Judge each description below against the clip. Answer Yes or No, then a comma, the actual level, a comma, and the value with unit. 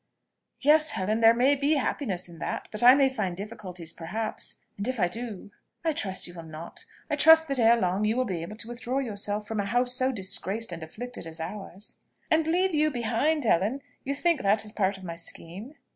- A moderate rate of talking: No, fast, 220 wpm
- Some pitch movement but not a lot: No, wide, 5.7 semitones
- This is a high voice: Yes, high, 220 Hz